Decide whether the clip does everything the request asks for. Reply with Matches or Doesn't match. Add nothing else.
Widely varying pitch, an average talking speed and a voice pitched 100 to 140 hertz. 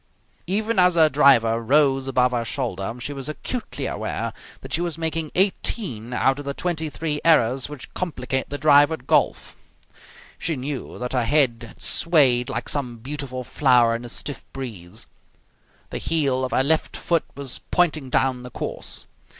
Doesn't match